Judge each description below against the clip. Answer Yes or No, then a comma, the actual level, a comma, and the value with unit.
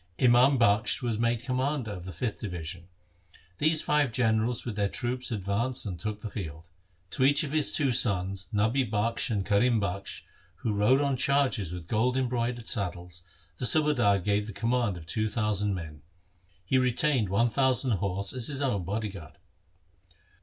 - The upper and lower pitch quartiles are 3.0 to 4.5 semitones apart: Yes, average, 4.2 semitones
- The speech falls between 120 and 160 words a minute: No, average, 170 wpm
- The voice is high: No, low, 110 Hz